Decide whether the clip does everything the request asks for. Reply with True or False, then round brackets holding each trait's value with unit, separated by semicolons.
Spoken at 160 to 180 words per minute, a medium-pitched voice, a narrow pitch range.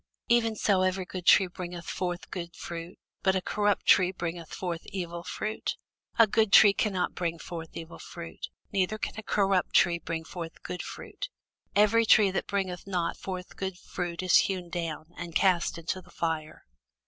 True (175 wpm; 180 Hz; 2.3 semitones)